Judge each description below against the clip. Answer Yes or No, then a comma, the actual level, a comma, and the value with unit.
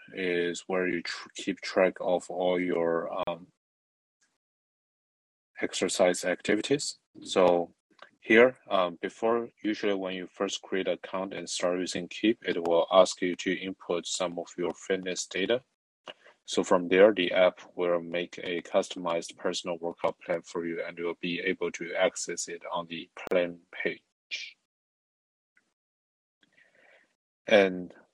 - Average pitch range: No, narrow, 1.5 semitones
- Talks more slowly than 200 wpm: Yes, slow, 135 wpm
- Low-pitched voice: Yes, very low, 90 Hz